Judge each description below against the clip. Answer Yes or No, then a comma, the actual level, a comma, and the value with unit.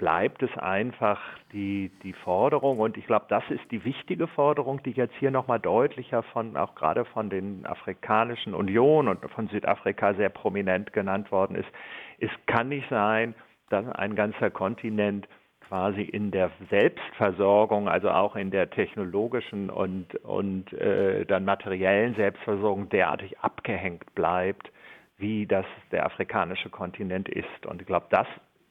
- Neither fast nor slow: Yes, average, 150 wpm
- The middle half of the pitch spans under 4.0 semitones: Yes, average, 3.2 semitones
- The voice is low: Yes, low, 105 Hz